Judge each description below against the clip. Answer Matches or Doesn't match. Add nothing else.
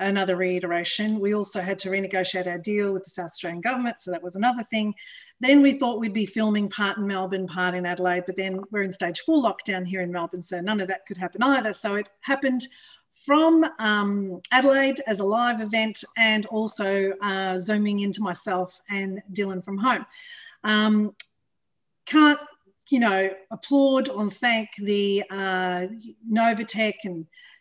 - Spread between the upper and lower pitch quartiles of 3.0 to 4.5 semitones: Matches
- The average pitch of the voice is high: Matches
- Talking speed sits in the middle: Matches